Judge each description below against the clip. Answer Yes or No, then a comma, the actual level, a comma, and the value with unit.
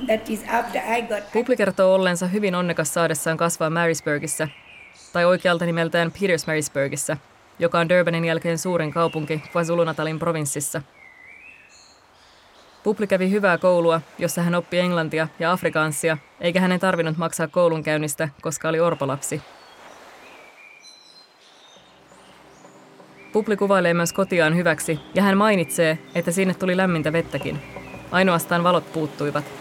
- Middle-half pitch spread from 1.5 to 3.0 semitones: Yes, narrow, 2.4 semitones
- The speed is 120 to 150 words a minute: No, average, 110 wpm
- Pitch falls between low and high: Yes, medium, 170 Hz